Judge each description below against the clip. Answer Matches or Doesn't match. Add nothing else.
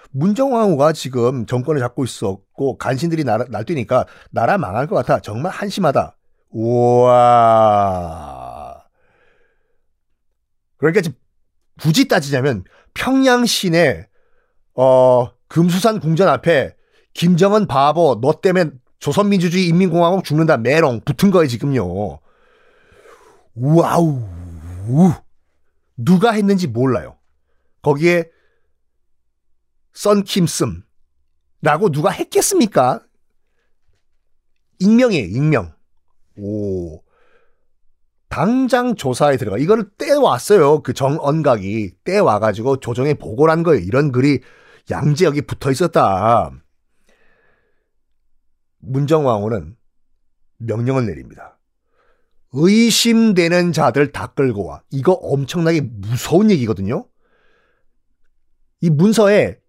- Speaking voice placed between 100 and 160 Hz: Matches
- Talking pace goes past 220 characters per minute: Doesn't match